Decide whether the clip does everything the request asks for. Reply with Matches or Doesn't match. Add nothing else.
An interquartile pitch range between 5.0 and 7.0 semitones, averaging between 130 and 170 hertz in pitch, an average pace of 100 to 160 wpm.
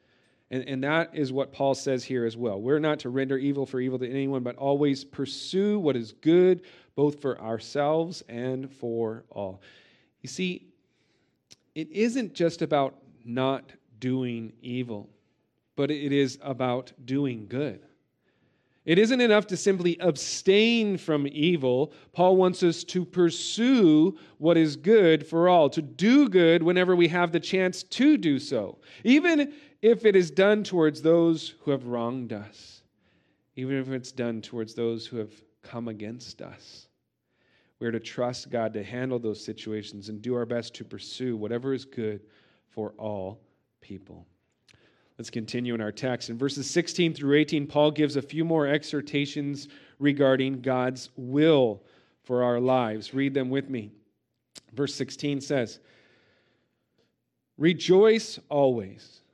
Matches